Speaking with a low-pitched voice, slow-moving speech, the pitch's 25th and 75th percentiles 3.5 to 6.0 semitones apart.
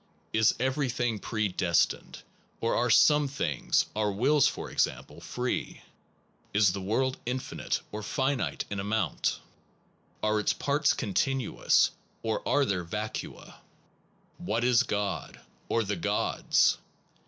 Yes: low, 110 Hz; slow, 120 wpm; average, 4.1 semitones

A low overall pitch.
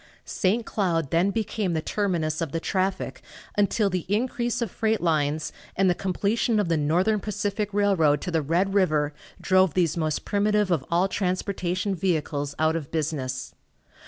No: medium, 185 Hz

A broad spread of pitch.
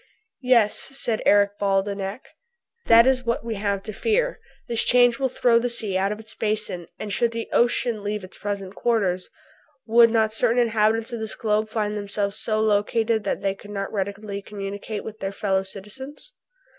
No: narrow, 2.6 semitones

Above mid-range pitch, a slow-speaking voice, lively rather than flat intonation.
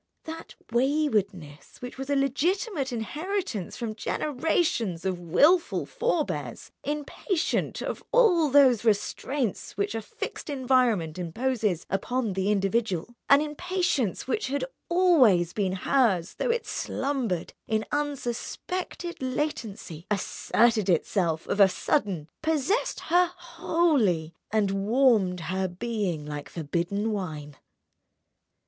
Yes: high, 235 Hz; slow, 110 wpm; wide, 7.8 semitones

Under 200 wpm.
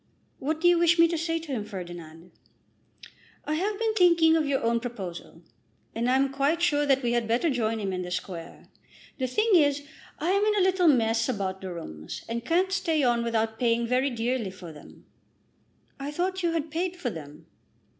No: fast, 205 wpm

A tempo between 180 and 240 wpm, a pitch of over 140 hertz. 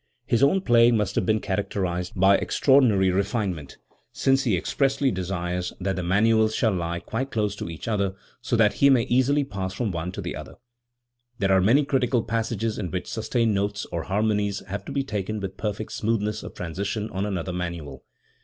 No: average, 190 wpm; low, 105 Hz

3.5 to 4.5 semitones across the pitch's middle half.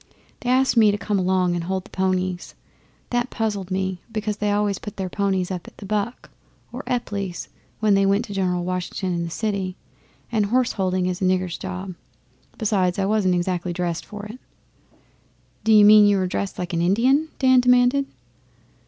No: average, 2.7 semitones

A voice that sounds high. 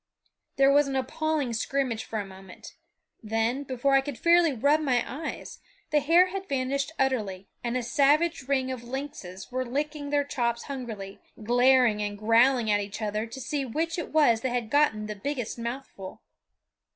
Yes: very high, 255 Hz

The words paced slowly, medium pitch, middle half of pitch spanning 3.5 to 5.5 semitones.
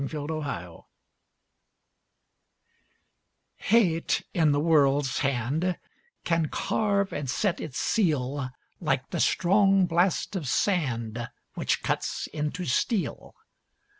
Yes: slow, 105 wpm; medium, 155 Hz; average, 5.1 semitones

